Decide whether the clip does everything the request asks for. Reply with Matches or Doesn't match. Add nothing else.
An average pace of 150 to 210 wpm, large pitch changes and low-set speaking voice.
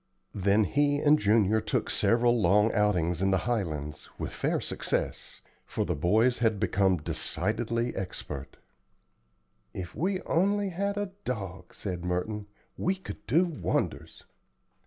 Doesn't match